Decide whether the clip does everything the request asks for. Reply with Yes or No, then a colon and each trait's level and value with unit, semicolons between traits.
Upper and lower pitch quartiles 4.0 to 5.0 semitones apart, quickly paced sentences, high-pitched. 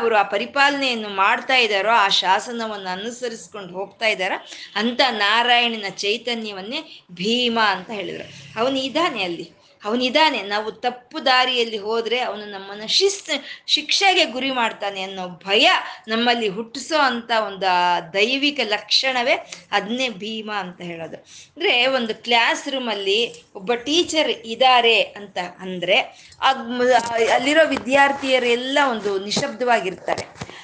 Yes: average, 4.5 semitones; fast, 110 wpm; high, 235 Hz